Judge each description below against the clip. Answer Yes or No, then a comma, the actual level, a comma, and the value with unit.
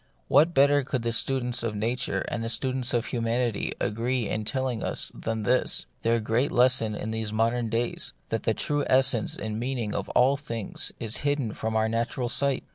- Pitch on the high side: No, low, 120 Hz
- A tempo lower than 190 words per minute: No, average, 200 wpm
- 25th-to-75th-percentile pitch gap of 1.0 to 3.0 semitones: Yes, narrow, 2.6 semitones